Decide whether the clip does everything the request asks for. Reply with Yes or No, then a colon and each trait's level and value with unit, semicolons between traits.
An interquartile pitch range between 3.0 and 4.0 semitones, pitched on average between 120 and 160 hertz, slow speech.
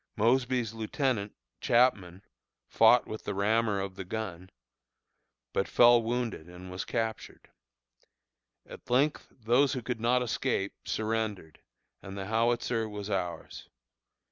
No: average, 3.6 semitones; low, 110 Hz; slow, 120 wpm